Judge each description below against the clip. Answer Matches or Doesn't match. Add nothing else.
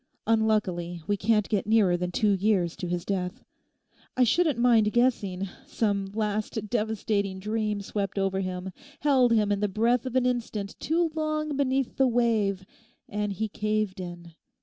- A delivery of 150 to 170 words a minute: Matches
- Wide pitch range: Doesn't match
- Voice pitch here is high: Matches